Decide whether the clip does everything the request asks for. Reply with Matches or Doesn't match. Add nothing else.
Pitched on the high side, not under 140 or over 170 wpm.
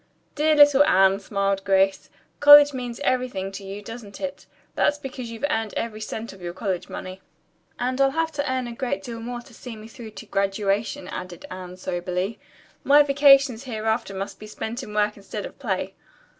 Doesn't match